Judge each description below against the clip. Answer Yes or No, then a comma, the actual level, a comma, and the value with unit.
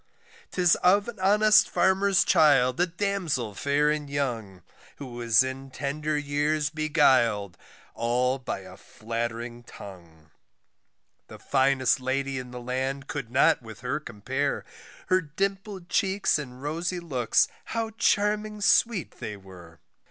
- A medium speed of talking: No, slow, 130 wpm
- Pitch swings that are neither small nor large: No, wide, 6.5 semitones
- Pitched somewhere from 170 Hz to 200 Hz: No, medium, 140 Hz